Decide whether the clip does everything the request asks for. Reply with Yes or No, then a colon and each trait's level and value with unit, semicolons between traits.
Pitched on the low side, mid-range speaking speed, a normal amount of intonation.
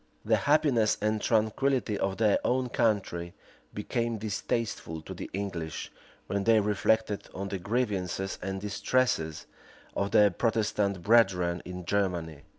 No: low, 105 Hz; slow, 130 wpm; average, 3.2 semitones